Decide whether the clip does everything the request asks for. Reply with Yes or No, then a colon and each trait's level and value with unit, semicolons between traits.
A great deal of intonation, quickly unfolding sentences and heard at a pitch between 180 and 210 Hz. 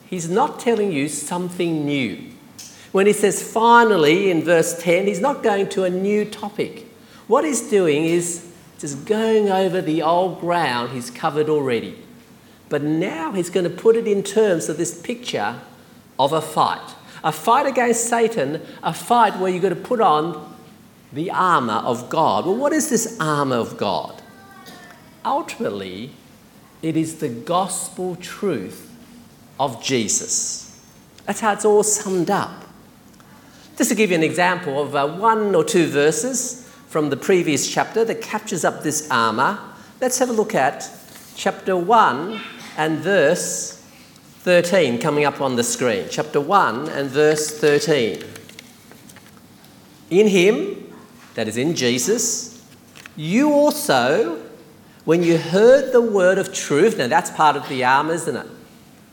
No: wide, 5.8 semitones; average, 150 wpm; medium, 185 Hz